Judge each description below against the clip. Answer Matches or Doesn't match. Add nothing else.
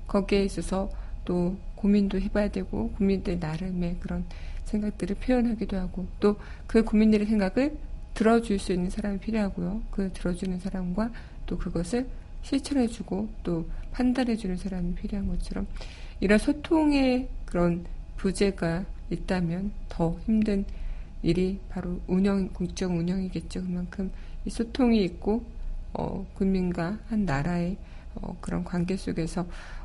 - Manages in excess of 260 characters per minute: Matches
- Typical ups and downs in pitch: Matches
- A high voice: Matches